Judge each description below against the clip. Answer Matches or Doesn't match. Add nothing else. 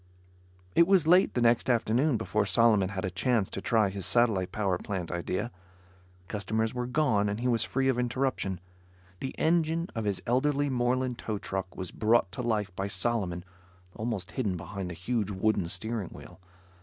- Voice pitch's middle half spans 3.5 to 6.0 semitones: Matches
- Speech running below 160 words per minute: Doesn't match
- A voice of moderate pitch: Doesn't match